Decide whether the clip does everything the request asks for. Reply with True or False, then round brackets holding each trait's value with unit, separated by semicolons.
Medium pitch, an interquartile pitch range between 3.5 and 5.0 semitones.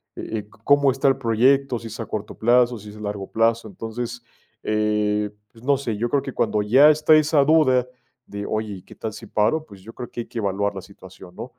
False (115 Hz; 3.9 semitones)